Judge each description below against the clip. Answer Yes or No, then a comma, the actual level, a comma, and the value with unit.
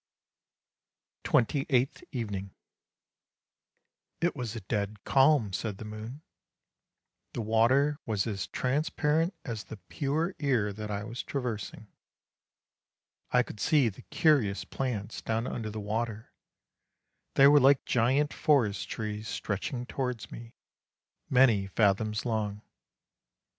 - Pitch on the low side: Yes, low, 115 Hz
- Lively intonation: No, average, 4.2 semitones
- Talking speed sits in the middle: No, slow, 125 wpm